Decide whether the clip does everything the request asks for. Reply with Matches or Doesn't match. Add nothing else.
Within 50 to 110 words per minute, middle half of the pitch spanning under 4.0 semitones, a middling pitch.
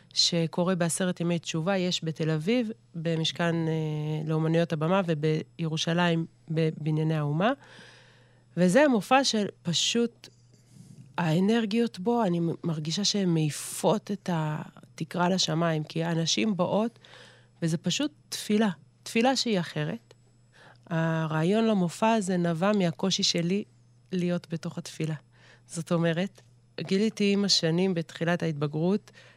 Matches